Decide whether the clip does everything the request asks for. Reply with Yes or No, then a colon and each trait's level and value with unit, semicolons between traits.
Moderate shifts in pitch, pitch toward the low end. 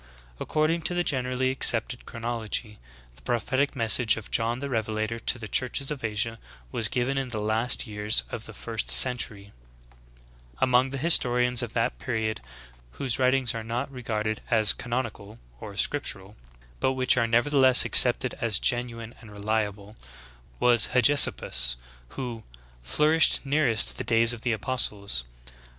Yes: average, 3.0 semitones; low, 120 Hz